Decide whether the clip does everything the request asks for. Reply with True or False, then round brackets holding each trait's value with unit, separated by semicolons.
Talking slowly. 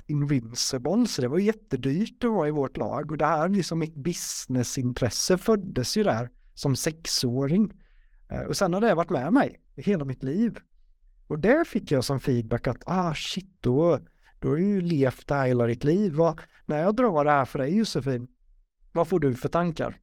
False (190 wpm)